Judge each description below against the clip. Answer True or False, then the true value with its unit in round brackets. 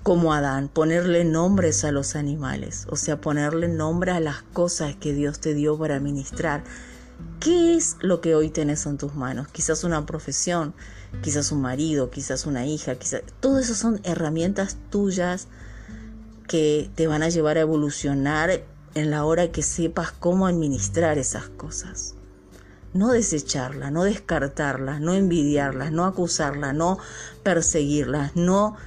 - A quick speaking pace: False (150 wpm)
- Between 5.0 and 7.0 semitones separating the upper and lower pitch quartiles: False (3.6 semitones)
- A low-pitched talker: False (150 Hz)